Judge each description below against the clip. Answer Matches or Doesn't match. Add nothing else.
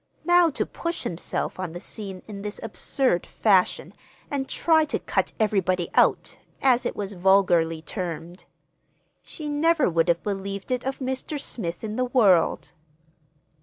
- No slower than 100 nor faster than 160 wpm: Matches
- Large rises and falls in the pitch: Matches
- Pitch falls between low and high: Doesn't match